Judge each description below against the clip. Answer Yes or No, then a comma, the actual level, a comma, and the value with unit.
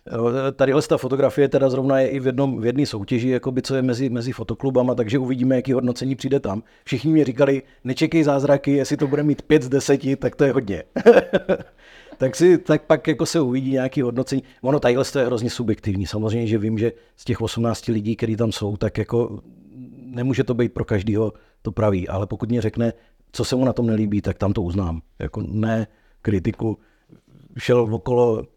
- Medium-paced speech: No, fast, 200 wpm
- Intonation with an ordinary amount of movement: Yes, average, 3.3 semitones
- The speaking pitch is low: Yes, low, 125 Hz